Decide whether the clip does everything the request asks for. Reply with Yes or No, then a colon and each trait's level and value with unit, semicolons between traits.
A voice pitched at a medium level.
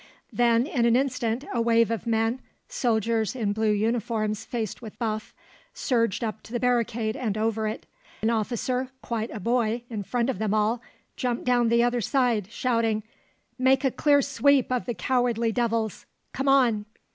No: high, 230 Hz